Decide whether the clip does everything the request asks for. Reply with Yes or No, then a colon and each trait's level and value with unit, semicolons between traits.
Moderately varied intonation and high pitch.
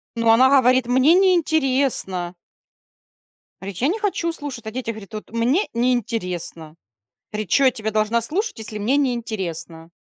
Yes: average, 4.4 semitones; high, 235 Hz